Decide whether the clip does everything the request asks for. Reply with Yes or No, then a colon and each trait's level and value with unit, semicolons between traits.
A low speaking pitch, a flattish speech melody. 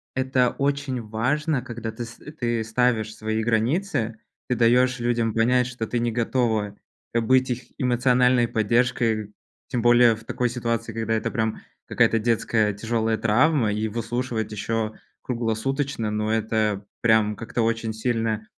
Yes: low, 115 Hz; narrow, 2.0 semitones